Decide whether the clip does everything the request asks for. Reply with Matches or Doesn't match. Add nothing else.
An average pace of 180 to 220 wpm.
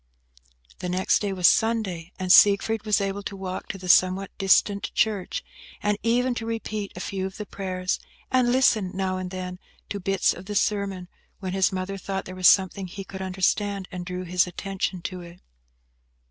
Matches